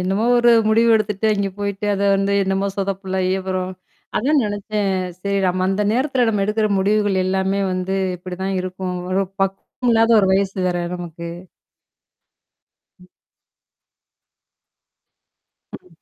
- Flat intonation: Yes, narrow, 2.0 semitones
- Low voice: No, high, 195 Hz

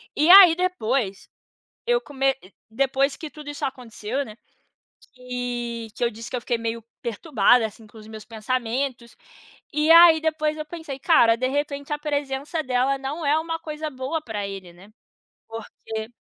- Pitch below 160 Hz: No, very high, 265 Hz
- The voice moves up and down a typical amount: Yes, average, 4.8 semitones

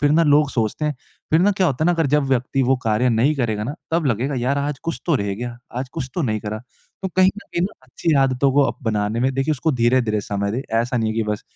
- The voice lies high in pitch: No, low, 130 Hz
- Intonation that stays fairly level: No, average, 4.4 semitones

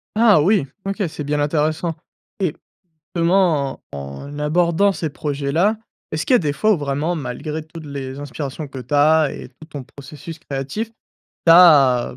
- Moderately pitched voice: Yes, medium, 150 Hz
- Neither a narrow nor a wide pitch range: Yes, average, 3.5 semitones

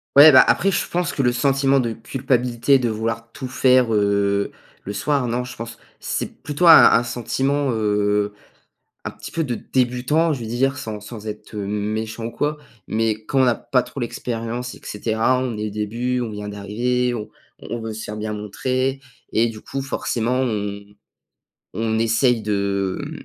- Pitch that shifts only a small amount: No, average, 3.3 semitones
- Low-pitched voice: Yes, low, 115 Hz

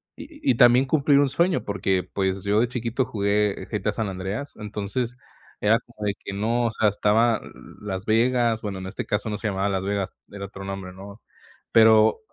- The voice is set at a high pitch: No, low, 105 Hz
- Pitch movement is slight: No, average, 3.2 semitones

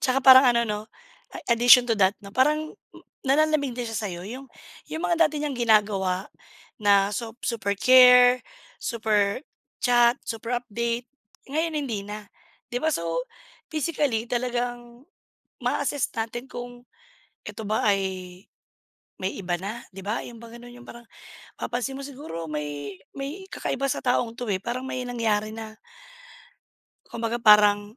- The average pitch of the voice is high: Yes, high, 235 Hz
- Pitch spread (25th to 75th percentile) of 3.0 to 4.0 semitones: Yes, average, 3.5 semitones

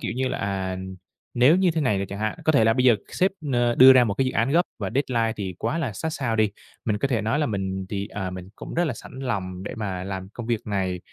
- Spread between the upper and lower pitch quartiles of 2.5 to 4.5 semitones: No, average, 4.9 semitones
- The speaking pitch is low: Yes, low, 110 Hz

